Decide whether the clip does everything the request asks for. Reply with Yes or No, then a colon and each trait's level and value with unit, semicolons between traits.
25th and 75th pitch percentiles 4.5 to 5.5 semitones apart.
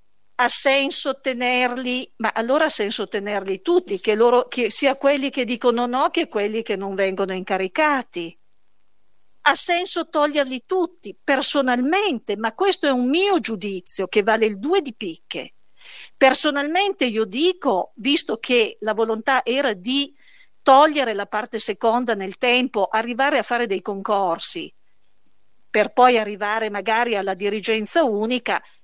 Yes: average, 4.9 semitones